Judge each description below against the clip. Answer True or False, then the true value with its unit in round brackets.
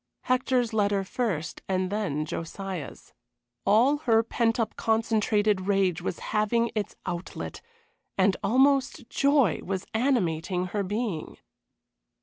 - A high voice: True (210 Hz)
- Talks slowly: True (115 wpm)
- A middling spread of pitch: True (3.8 semitones)